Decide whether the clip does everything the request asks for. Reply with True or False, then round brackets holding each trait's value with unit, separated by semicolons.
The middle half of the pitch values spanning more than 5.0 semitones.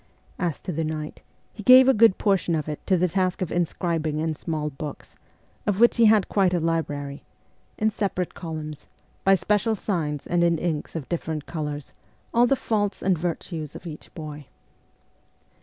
False (4.1 semitones)